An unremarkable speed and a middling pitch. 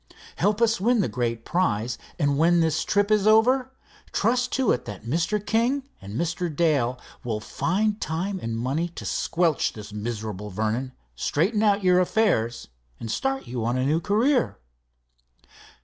Yes: average, 160 wpm; medium, 170 Hz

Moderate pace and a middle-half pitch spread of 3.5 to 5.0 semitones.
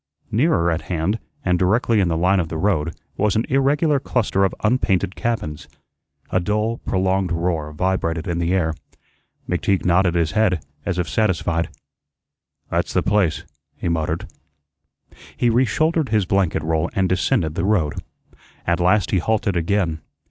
Yes: average, 155 wpm; average, 4.1 semitones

